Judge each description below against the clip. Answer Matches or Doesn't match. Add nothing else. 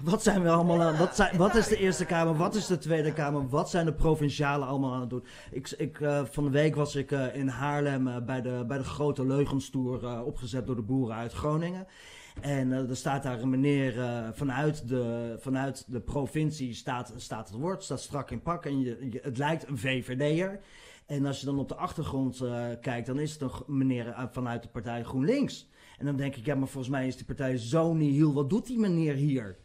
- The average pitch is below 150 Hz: Matches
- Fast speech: Matches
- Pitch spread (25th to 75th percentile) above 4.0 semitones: Doesn't match